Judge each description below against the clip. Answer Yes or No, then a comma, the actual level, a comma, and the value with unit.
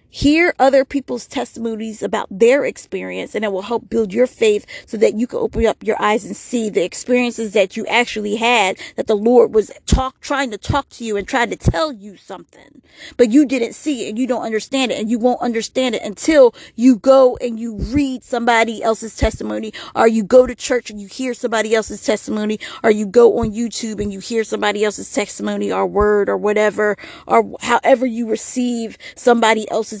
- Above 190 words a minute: Yes, fast, 205 wpm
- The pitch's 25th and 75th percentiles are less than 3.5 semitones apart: Yes, average, 2.9 semitones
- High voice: Yes, high, 230 Hz